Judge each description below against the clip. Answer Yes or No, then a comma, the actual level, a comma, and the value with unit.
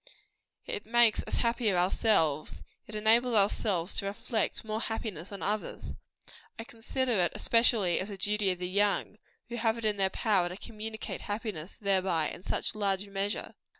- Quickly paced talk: No, average, 165 wpm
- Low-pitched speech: No, high, 210 Hz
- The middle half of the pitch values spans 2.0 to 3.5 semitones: Yes, average, 2.8 semitones